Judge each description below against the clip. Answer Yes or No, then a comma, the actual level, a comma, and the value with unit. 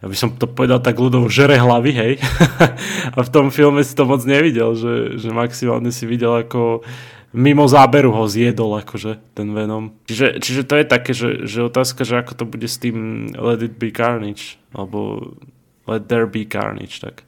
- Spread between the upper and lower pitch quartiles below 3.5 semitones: Yes, average, 2.7 semitones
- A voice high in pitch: No, low, 120 Hz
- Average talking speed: No, fast, 190 wpm